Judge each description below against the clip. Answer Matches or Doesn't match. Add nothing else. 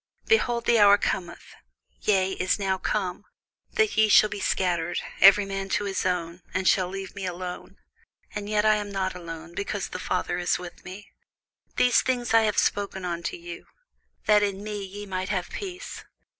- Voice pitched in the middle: Doesn't match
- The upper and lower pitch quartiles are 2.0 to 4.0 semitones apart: Matches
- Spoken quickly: Doesn't match